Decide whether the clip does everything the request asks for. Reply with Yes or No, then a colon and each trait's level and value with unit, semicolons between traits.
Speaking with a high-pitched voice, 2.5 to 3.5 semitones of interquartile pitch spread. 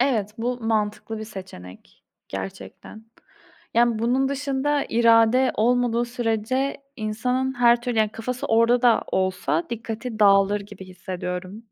Yes: high, 225 Hz; average, 3.1 semitones